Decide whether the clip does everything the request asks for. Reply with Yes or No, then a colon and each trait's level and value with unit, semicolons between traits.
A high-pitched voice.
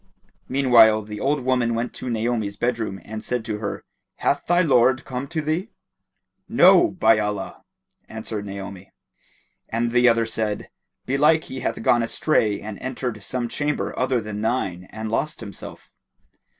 No: low, 115 Hz